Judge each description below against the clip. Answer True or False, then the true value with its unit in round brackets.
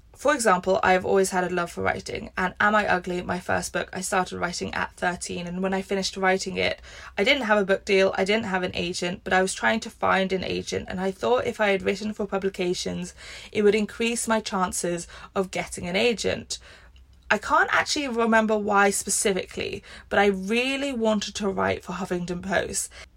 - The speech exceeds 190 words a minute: True (205 wpm)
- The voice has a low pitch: False (190 Hz)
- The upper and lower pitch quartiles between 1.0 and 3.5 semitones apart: True (2.9 semitones)